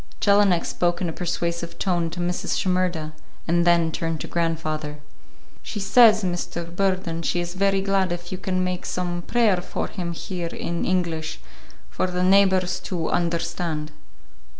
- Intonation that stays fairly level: Yes, narrow, 1.7 semitones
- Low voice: No, medium, 175 Hz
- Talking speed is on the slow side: No, average, 155 wpm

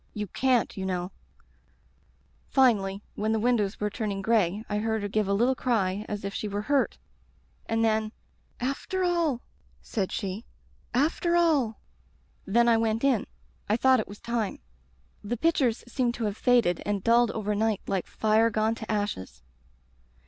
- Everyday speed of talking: Yes, average, 165 wpm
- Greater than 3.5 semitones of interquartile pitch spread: No, average, 2.8 semitones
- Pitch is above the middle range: Yes, high, 220 Hz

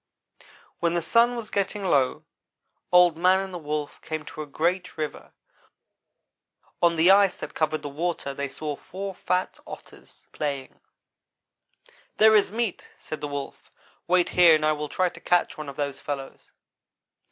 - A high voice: No, medium, 165 Hz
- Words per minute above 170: No, average, 165 wpm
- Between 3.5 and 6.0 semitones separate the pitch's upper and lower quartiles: Yes, average, 3.9 semitones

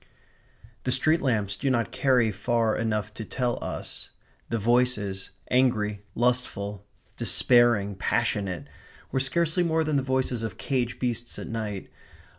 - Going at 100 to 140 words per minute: Yes, slow, 135 wpm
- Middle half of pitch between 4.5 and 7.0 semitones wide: No, average, 3.6 semitones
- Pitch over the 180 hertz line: No, low, 120 Hz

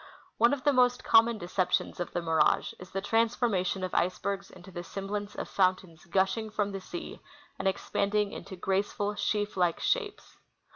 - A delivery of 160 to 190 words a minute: Yes, average, 175 wpm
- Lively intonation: No, average, 3.0 semitones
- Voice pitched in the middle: No, high, 200 Hz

